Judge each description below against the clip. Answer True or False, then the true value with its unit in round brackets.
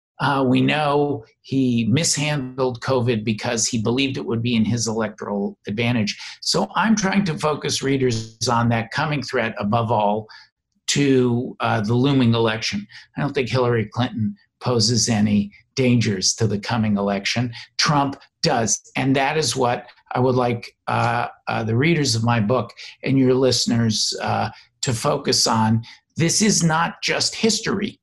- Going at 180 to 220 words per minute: False (155 wpm)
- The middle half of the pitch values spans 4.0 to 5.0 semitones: False (3.3 semitones)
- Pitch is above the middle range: False (120 Hz)